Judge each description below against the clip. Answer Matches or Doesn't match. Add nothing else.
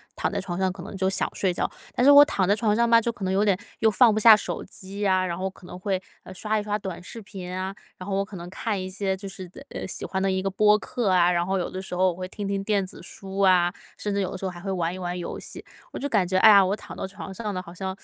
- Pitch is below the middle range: Doesn't match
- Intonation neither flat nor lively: Doesn't match